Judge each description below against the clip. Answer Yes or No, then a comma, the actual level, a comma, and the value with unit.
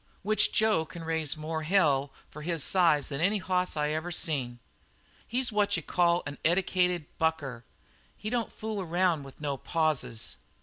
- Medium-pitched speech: Yes, medium, 165 Hz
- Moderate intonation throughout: Yes, average, 3.7 semitones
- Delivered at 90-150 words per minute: No, average, 165 wpm